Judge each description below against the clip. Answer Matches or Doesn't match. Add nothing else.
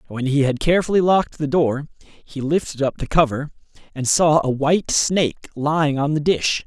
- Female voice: Doesn't match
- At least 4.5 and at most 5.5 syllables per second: Matches